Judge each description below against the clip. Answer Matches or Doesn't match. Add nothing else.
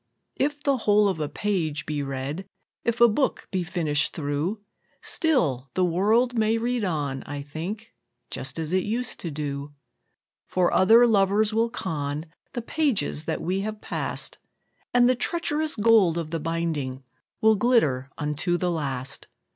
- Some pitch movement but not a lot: Doesn't match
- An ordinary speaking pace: Matches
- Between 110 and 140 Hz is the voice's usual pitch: Doesn't match